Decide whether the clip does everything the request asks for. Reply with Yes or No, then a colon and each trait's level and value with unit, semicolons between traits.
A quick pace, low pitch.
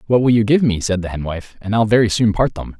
Yes: fast, 320 wpm; low, 105 Hz